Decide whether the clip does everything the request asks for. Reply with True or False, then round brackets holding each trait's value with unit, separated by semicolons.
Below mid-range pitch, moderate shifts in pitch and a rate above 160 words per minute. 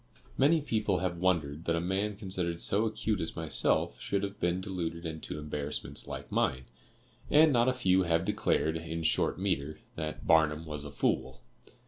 True (85 Hz; 4.1 semitones; 170 wpm)